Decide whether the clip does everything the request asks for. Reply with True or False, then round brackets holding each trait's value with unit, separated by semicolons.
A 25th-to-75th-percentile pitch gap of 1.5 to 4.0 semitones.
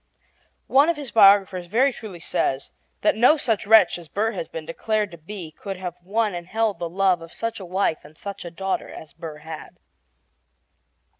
False (4.4 semitones)